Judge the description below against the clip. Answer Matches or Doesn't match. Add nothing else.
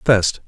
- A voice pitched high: Doesn't match